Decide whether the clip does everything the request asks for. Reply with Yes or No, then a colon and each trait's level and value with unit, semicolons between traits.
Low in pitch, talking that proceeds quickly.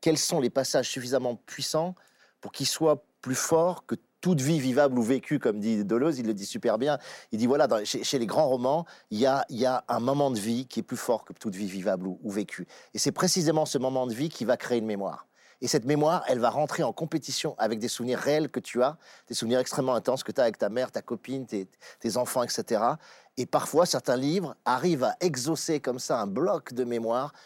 Yes: low, 130 Hz; fast, 240 wpm